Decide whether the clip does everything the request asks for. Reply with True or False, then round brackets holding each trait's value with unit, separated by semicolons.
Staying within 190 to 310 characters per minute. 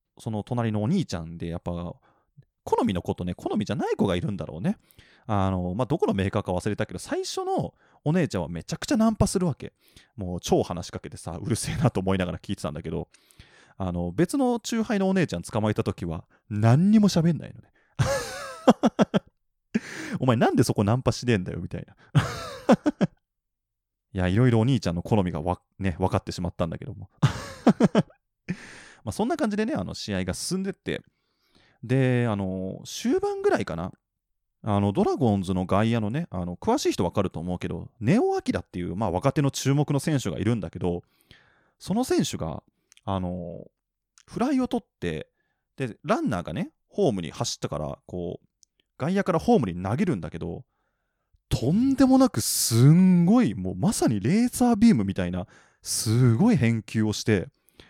False (360 characters per minute)